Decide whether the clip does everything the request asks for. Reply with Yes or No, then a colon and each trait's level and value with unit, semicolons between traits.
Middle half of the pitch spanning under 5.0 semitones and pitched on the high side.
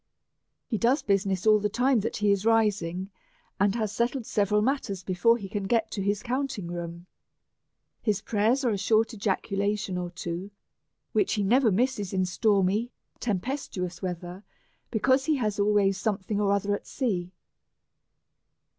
Yes: average, 3.0 semitones; high, 205 Hz